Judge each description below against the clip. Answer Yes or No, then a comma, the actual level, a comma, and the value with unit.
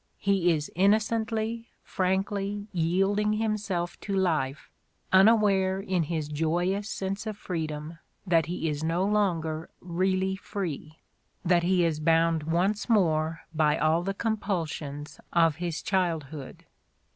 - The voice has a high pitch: No, medium, 180 Hz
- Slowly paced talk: Yes, slow, 120 wpm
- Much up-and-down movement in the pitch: No, average, 3.6 semitones